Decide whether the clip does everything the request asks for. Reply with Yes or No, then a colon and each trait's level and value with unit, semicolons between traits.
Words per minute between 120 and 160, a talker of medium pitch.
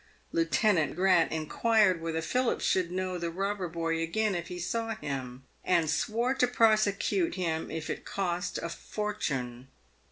Yes: average, 155 wpm; medium, 180 Hz